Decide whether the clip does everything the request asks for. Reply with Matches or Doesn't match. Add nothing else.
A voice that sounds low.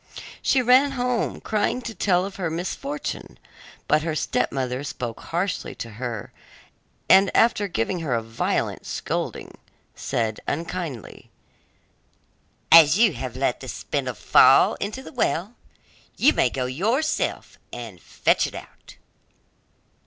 Doesn't match